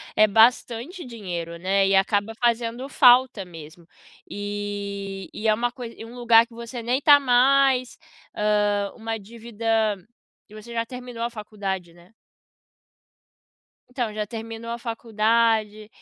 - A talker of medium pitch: No, high, 225 Hz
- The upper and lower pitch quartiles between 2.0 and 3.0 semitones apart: Yes, average, 2.7 semitones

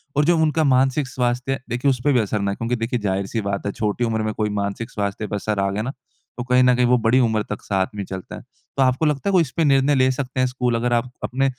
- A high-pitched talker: No, low, 120 Hz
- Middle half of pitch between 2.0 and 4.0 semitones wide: Yes, average, 3.7 semitones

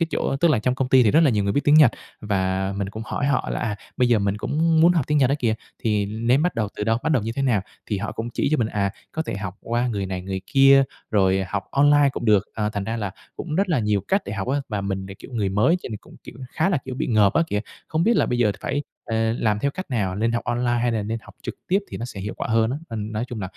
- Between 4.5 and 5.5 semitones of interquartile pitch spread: Yes, average, 5.0 semitones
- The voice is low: Yes, low, 115 Hz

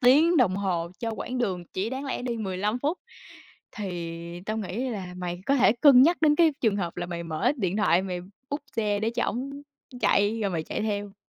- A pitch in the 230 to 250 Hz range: No, high, 210 Hz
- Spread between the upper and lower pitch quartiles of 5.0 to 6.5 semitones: Yes, wide, 5.5 semitones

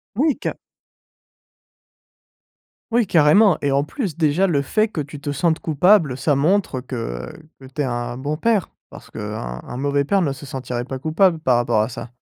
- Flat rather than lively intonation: No, wide, 5.6 semitones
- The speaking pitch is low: No, medium, 145 Hz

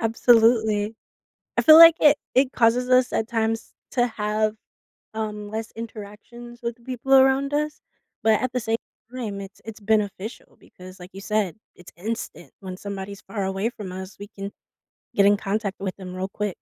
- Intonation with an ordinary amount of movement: Yes, average, 3.1 semitones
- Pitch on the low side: No, high, 220 Hz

